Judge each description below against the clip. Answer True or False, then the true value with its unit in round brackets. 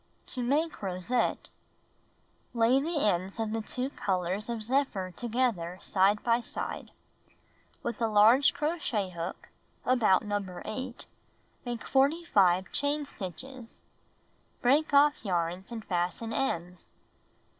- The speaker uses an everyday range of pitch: False (5.8 semitones)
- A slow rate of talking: True (115 wpm)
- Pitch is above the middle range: True (225 Hz)